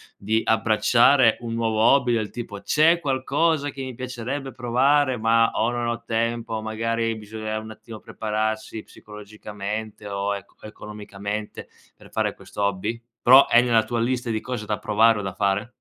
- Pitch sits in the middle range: No, low, 115 Hz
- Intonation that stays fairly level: Yes, narrow, 2.3 semitones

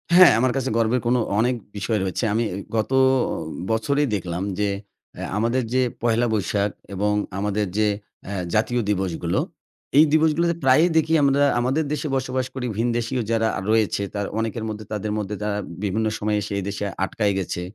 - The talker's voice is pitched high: No, low, 110 Hz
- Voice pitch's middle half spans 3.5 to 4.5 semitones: Yes, average, 3.8 semitones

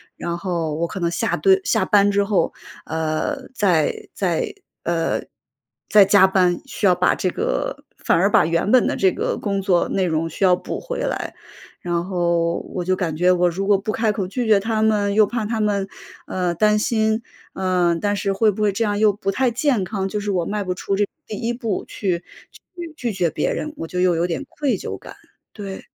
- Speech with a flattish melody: No, average, 3.4 semitones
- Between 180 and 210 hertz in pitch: Yes, high, 195 Hz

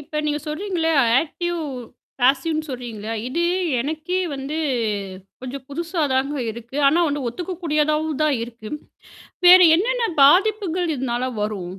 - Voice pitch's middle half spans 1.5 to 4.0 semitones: No, average, 4.7 semitones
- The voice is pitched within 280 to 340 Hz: Yes, very high, 300 Hz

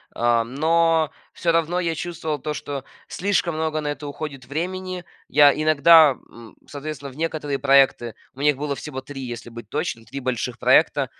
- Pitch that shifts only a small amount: No, average, 3.5 semitones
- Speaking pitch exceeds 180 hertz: No, medium, 145 Hz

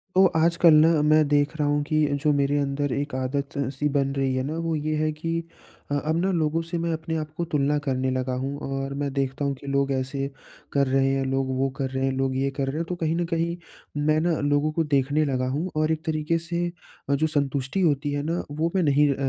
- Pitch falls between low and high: Yes, medium, 145 Hz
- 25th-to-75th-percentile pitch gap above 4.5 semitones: No, narrow, 2.5 semitones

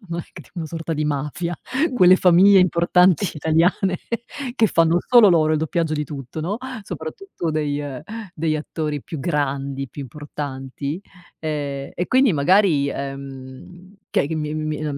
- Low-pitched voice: No, medium, 155 Hz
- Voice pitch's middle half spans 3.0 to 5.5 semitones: Yes, average, 3.6 semitones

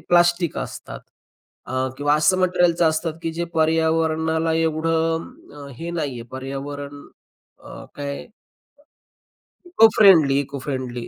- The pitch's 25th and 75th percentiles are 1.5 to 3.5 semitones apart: Yes, average, 2.7 semitones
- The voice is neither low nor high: Yes, medium, 160 Hz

